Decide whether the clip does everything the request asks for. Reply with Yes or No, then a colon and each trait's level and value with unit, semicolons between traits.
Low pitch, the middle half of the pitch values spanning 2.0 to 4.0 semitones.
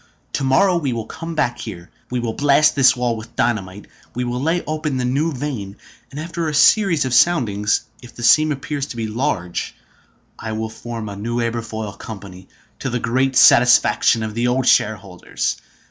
No: low, 120 Hz; average, 4.4 semitones